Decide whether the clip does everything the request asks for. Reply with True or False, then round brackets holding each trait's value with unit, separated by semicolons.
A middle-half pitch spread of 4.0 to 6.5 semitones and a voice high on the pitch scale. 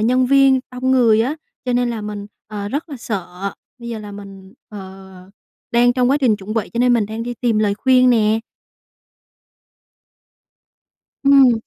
False (3.3 semitones; 230 Hz)